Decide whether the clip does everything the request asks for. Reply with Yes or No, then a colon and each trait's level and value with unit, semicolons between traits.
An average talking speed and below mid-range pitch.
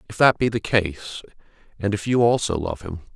No: fast, 210 wpm; low, 100 Hz